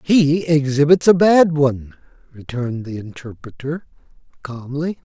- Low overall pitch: No, medium, 145 Hz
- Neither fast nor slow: No, slow, 105 wpm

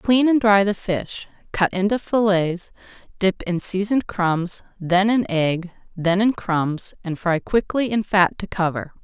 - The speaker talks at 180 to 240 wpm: No, average, 165 wpm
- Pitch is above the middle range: Yes, high, 195 Hz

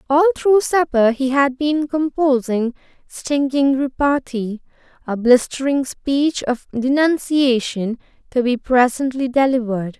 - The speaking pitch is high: Yes, very high, 270 Hz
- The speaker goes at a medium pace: No, slow, 110 wpm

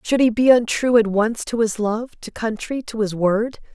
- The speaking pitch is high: Yes, high, 225 Hz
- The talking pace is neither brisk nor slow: No, fast, 225 wpm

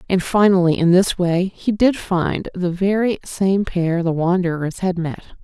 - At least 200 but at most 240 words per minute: No, average, 175 wpm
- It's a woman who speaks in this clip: Yes, female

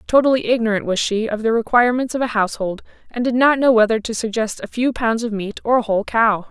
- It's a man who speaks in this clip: No, female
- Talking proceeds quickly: Yes, fast, 240 wpm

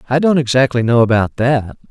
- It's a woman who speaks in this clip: No, male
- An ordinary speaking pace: Yes, average, 190 wpm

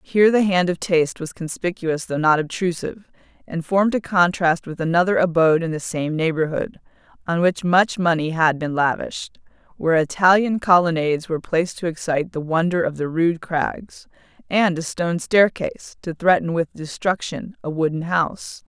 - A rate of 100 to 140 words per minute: No, average, 165 wpm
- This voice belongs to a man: No, female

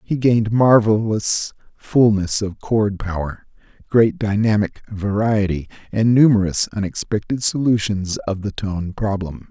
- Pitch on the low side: Yes, low, 105 Hz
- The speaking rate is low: Yes, slow, 115 wpm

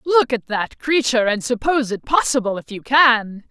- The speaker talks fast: No, average, 190 wpm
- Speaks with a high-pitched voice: Yes, high, 245 Hz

